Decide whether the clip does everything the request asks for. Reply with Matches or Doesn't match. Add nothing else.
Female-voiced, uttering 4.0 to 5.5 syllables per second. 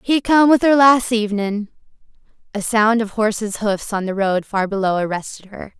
Matches